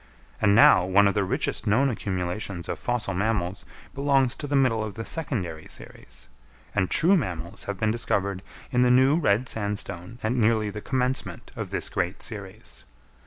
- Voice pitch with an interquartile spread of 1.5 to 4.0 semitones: No, average, 4.5 semitones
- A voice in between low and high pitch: No, low, 105 Hz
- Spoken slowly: No, average, 170 wpm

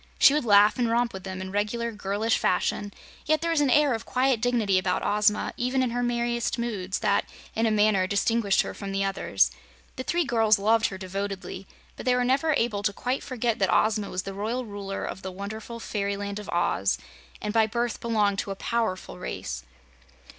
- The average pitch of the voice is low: No, high, 215 Hz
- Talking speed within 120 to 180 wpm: No, fast, 205 wpm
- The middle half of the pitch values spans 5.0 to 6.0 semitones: No, average, 3.3 semitones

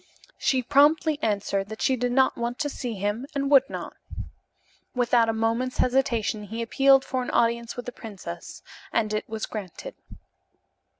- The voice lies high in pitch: Yes, high, 235 Hz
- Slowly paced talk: No, average, 165 wpm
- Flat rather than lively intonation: No, average, 3.4 semitones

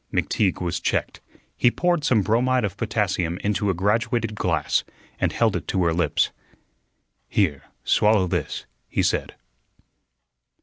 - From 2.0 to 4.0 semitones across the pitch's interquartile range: No, average, 4.5 semitones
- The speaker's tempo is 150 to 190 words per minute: No, slow, 135 wpm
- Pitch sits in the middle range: No, low, 105 Hz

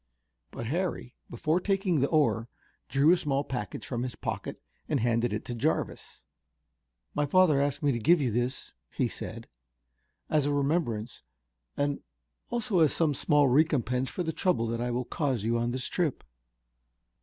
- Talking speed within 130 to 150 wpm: No, average, 165 wpm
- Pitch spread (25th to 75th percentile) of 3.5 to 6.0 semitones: Yes, average, 4.7 semitones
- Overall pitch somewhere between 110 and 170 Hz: Yes, medium, 140 Hz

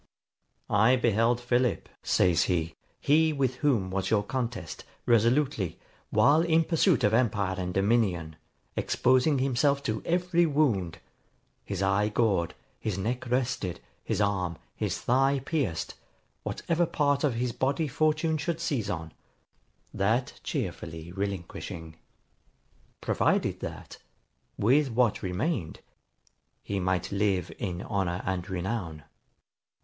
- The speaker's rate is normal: No, slow, 120 wpm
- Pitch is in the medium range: No, low, 115 Hz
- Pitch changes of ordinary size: No, wide, 6.5 semitones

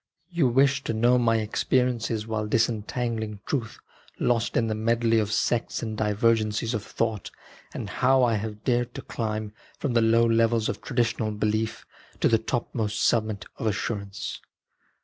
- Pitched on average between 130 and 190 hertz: No, low, 115 Hz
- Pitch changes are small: Yes, narrow, 1.6 semitones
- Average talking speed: Yes, average, 160 wpm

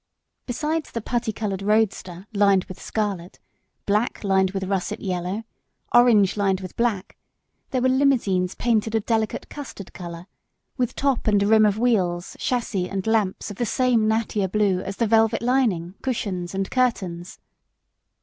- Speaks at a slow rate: No, average, 150 wpm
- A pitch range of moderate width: Yes, average, 3.6 semitones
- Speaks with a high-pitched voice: Yes, high, 210 Hz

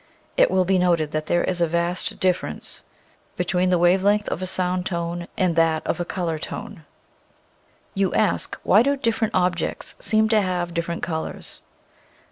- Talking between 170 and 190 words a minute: Yes, average, 175 wpm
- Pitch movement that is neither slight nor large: No, narrow, 1.7 semitones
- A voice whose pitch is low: No, medium, 180 Hz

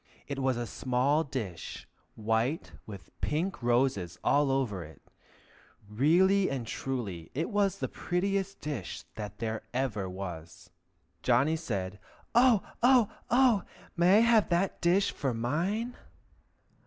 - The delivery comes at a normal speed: No, slow, 125 wpm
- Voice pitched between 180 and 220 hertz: No, low, 135 Hz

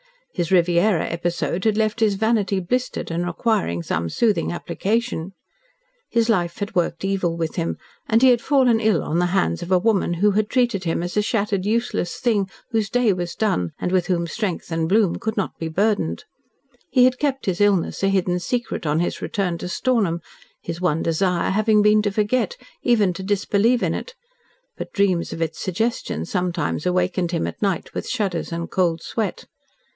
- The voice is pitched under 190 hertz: No, high, 195 Hz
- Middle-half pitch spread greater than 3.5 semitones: Yes, average, 4.2 semitones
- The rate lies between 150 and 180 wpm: No, average, 190 wpm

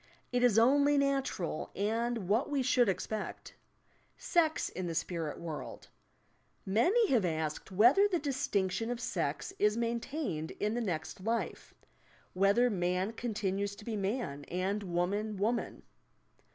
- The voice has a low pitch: No, high, 215 Hz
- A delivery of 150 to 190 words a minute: No, average, 140 wpm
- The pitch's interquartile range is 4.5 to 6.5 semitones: Yes, average, 4.8 semitones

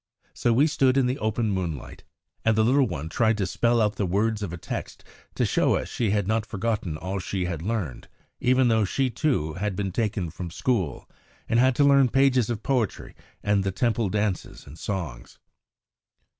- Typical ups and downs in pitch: Yes, average, 4.3 semitones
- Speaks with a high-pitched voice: No, low, 105 Hz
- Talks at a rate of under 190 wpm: No, average, 195 wpm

